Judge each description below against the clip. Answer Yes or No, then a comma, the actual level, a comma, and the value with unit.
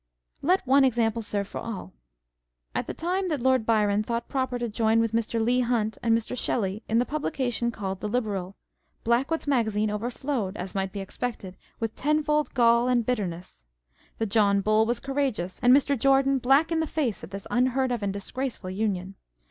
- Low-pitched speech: No, high, 230 Hz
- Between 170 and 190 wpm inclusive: Yes, average, 185 wpm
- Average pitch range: Yes, average, 4.0 semitones